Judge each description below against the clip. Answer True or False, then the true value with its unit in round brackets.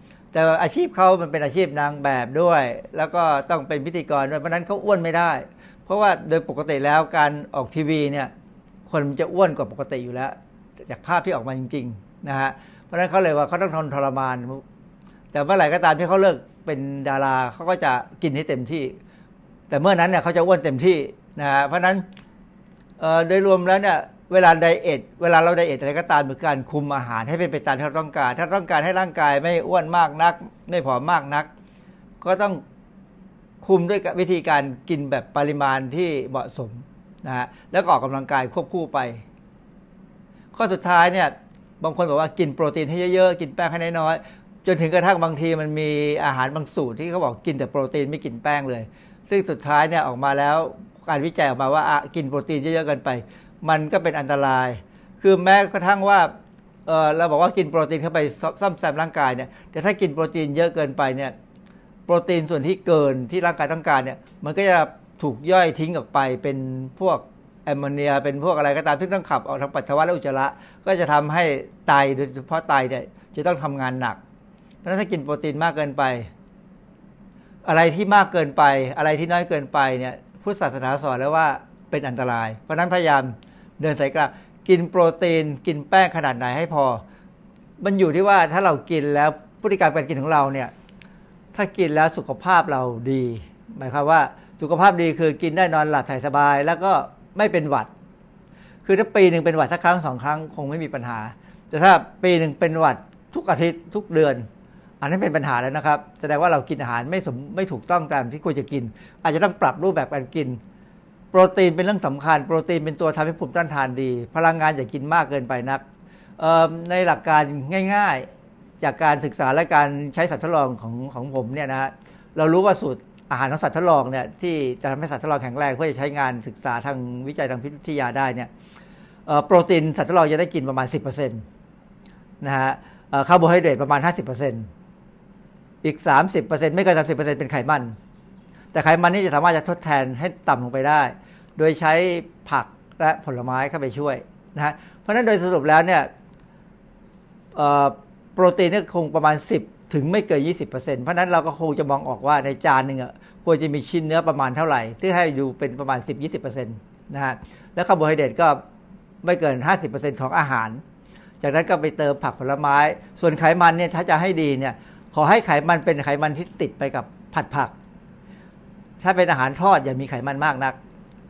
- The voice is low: False (160 Hz)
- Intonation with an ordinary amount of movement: True (4.8 semitones)